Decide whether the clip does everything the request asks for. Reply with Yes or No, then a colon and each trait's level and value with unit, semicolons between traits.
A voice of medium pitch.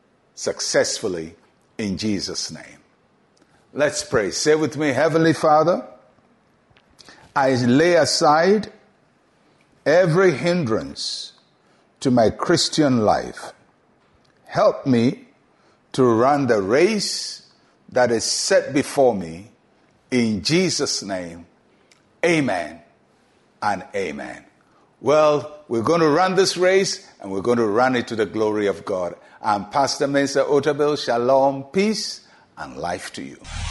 Yes: medium, 145 Hz